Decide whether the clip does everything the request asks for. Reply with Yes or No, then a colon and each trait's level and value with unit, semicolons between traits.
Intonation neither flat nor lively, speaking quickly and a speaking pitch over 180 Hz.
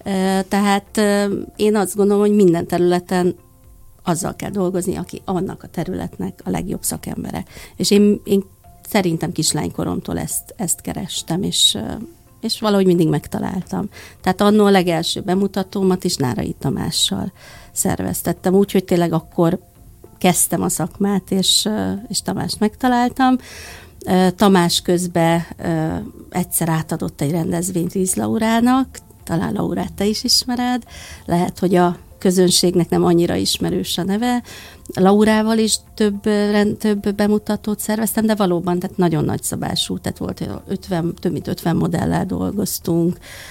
No: average, 3.1 semitones; average, 125 wpm; high, 190 Hz